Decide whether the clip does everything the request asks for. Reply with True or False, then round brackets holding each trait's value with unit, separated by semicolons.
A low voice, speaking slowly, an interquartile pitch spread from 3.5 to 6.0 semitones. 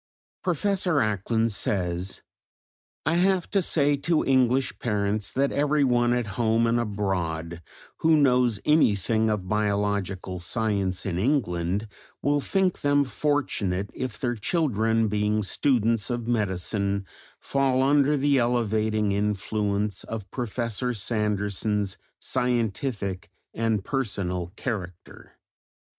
True (110 Hz; 110 wpm; 4.8 semitones)